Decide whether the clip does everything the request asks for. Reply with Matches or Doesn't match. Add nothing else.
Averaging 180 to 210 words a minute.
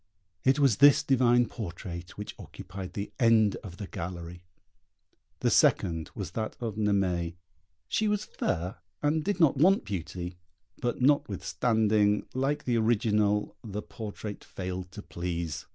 Doesn't match